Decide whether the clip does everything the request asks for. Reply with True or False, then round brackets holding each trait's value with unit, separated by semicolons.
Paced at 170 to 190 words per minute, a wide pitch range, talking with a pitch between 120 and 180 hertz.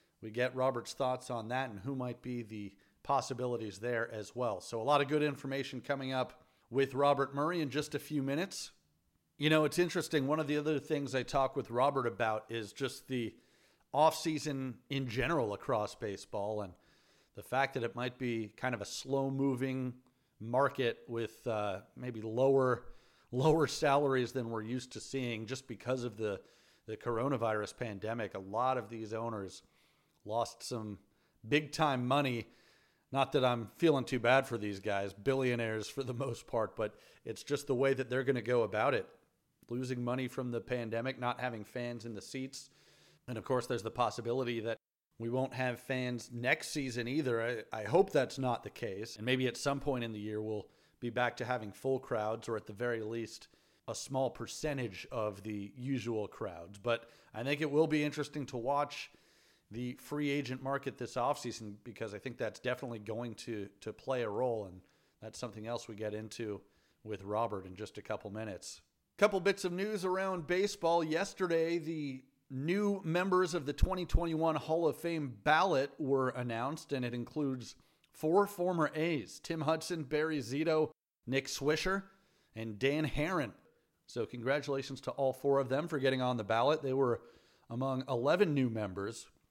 False (180 wpm; 3.7 semitones; 125 Hz)